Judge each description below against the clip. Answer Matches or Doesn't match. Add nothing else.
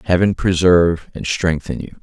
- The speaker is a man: Matches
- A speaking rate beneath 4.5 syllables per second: Doesn't match